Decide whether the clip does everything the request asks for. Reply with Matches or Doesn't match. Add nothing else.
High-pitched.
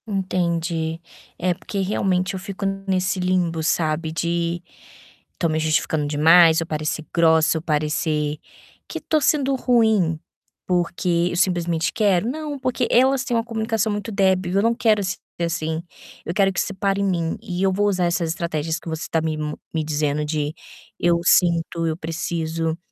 Doesn't match